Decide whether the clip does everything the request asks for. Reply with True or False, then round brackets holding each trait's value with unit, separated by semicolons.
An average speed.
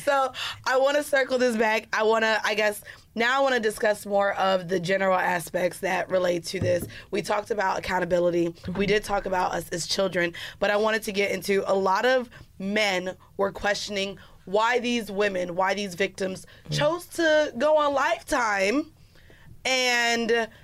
True (175 wpm)